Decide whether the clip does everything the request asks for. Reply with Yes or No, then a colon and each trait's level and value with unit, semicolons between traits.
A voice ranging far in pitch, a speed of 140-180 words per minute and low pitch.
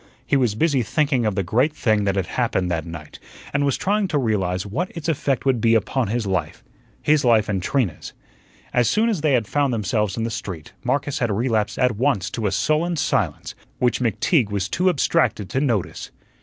No: wide, 6.0 semitones; fast, 205 wpm; low, 115 Hz